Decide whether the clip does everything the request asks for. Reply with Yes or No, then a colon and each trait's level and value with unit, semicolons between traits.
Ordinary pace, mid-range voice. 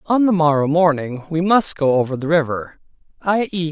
Yes: average, 195 wpm; medium, 160 Hz